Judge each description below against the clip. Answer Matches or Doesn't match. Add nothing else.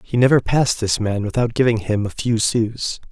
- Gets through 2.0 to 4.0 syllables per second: Doesn't match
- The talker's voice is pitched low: Matches